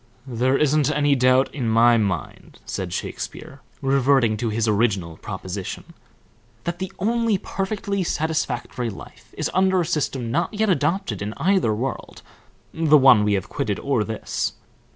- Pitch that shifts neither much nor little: No, wide, 7.3 semitones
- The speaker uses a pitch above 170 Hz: No, low, 135 Hz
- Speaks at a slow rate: No, average, 150 wpm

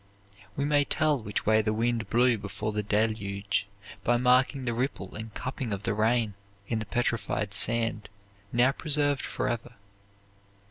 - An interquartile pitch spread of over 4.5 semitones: No, average, 2.9 semitones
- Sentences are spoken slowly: No, average, 150 wpm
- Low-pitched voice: Yes, low, 115 Hz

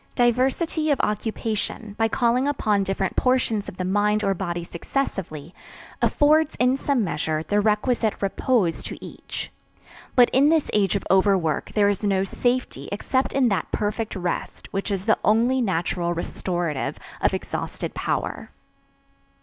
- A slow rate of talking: No, average, 145 wpm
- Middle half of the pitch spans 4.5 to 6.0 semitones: Yes, average, 4.8 semitones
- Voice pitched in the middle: No, high, 210 Hz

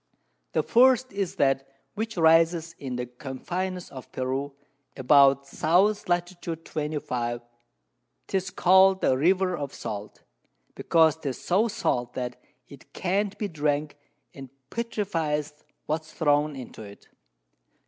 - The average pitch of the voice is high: No, medium, 155 Hz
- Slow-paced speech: Yes, slow, 120 wpm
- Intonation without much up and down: No, wide, 5.4 semitones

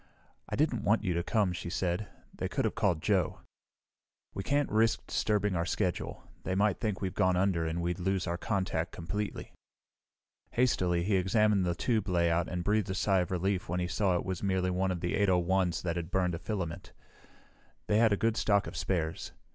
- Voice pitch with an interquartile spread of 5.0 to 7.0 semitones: No, average, 2.9 semitones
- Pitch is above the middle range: No, very low, 95 Hz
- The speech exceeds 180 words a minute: Yes, average, 200 wpm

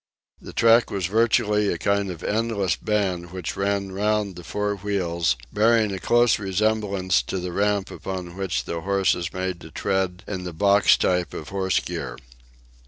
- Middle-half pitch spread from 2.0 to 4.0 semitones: Yes, narrow, 2.4 semitones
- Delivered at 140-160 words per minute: No, average, 170 wpm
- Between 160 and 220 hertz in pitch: No, very low, 95 Hz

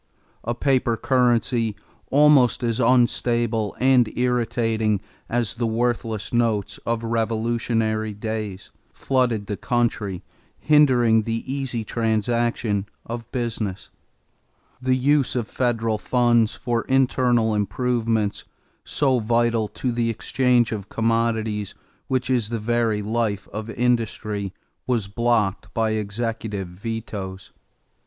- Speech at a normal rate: No, slow, 110 wpm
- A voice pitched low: Yes, low, 115 Hz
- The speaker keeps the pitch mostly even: Yes, narrow, 1.9 semitones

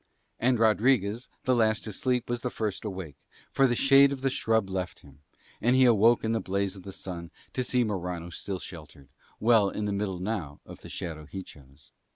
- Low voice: Yes, low, 105 Hz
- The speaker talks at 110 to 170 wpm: No, fast, 205 wpm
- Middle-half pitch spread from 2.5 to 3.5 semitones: No, average, 4.8 semitones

